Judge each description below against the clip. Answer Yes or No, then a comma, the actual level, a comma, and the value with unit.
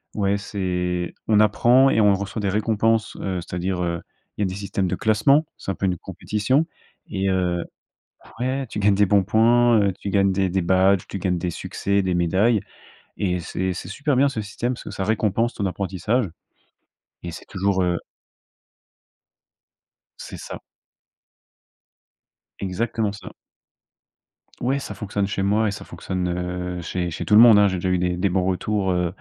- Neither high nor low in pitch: No, low, 100 Hz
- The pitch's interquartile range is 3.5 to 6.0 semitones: No, average, 2.9 semitones